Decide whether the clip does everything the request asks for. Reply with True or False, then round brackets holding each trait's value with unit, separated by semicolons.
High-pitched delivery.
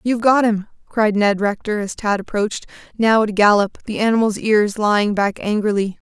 True (210 Hz)